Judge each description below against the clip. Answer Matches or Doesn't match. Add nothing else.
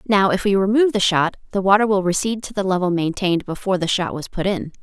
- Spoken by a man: Doesn't match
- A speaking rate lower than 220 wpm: Doesn't match